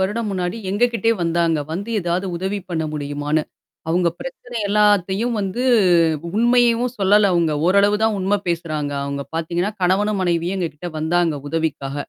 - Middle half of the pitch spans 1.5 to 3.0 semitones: No, average, 4.1 semitones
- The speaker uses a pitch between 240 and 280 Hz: No, medium, 185 Hz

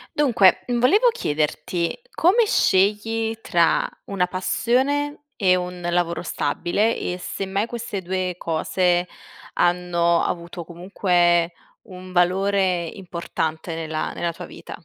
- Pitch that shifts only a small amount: No, average, 3.1 semitones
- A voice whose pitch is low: No, medium, 180 Hz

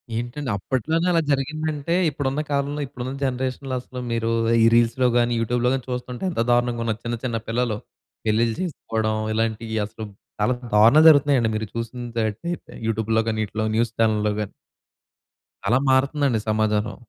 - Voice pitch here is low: Yes, low, 120 Hz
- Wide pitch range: No, average, 3.2 semitones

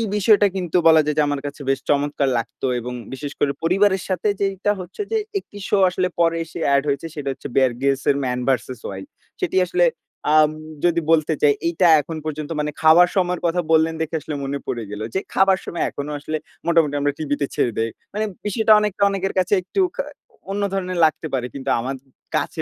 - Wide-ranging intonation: No, average, 4.5 semitones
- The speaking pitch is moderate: Yes, medium, 160 Hz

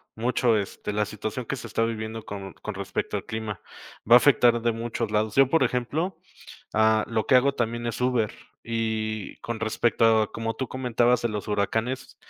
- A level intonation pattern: Yes, narrow, 2.0 semitones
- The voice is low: Yes, low, 115 Hz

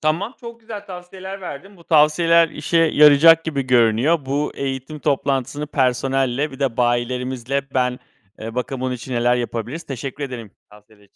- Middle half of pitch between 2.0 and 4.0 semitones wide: No, average, 4.5 semitones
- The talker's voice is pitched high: No, medium, 140 Hz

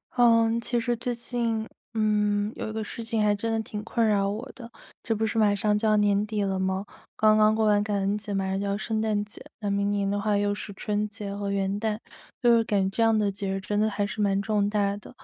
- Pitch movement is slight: Yes, narrow, 1.6 semitones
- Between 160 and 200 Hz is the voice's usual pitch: No, high, 210 Hz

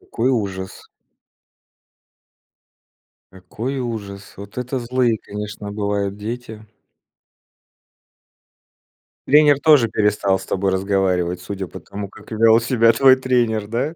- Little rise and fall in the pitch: No, average, 3.6 semitones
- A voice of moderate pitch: No, low, 110 Hz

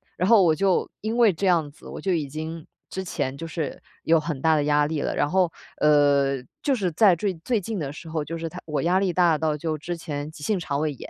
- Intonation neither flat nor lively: Yes, average, 3.5 semitones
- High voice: No, medium, 160 Hz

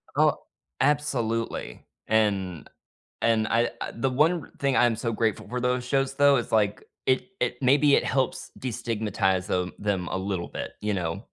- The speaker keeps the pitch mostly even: No, average, 4.3 semitones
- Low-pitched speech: Yes, low, 115 Hz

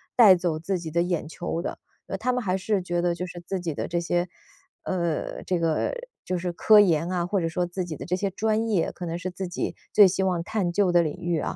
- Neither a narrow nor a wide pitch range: No, narrow, 1.9 semitones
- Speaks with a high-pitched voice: No, medium, 175 Hz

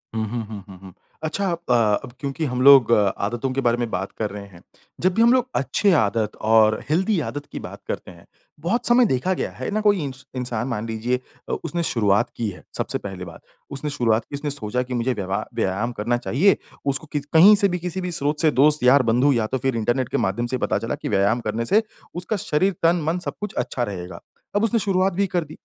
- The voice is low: Yes, low, 130 Hz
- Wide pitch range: Yes, wide, 7.7 semitones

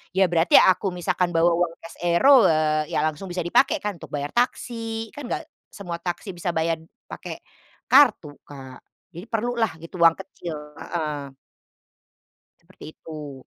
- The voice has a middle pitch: Yes, medium, 175 Hz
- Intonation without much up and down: No, average, 5.0 semitones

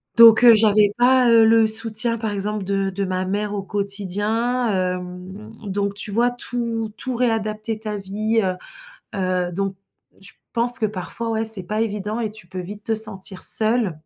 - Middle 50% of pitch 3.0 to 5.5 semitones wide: No, narrow, 2.4 semitones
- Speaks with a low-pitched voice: No, high, 215 Hz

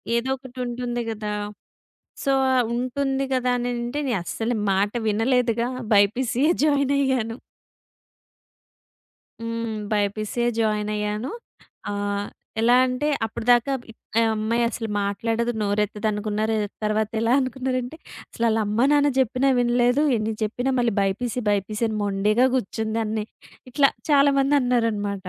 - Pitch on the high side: Yes, high, 230 Hz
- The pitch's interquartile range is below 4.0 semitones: Yes, average, 3.0 semitones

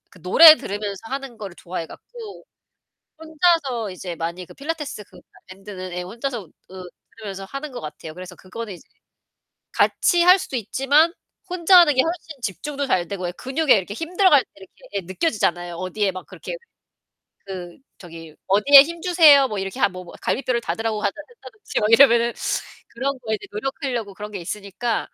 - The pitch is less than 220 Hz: No, high, 225 Hz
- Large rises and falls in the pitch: Yes, wide, 7.4 semitones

